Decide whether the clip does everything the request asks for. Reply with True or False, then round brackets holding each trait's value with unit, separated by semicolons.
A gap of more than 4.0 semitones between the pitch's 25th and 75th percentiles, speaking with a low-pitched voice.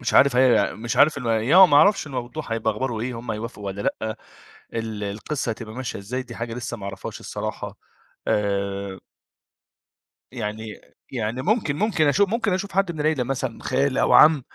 True (4.7 semitones; 120 Hz)